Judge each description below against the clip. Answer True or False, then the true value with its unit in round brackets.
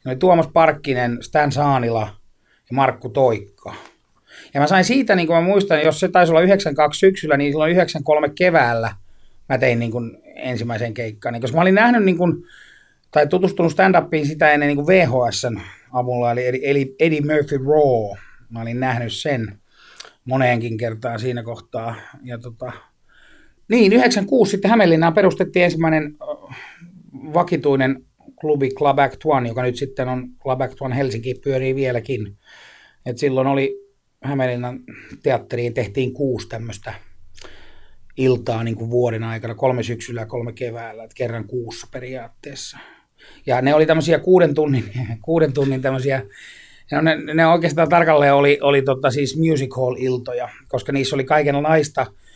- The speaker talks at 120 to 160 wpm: True (140 wpm)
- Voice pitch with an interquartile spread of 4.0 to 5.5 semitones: True (4.7 semitones)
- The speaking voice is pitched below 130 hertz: False (135 Hz)